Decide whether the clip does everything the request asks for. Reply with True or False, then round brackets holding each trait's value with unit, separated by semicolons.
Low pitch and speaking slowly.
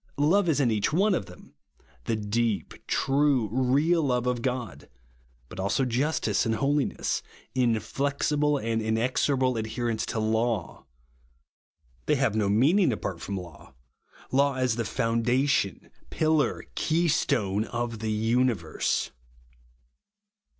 True (120 Hz; 115 wpm)